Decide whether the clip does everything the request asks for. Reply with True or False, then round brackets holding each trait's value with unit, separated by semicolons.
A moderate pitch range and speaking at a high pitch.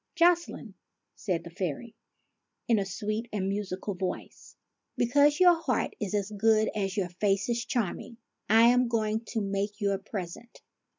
True (3.3 semitones; 215 Hz)